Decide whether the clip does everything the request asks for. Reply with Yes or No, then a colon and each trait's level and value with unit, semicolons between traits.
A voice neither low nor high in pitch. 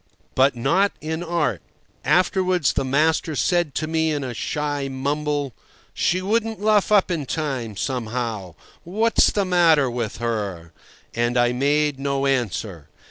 Yes: medium, 145 Hz